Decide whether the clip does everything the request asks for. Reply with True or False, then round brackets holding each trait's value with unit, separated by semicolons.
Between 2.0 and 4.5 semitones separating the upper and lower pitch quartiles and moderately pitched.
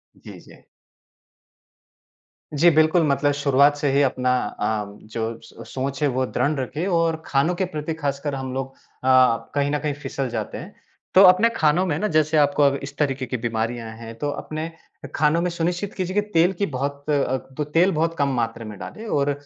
True (3.5 semitones; 145 Hz)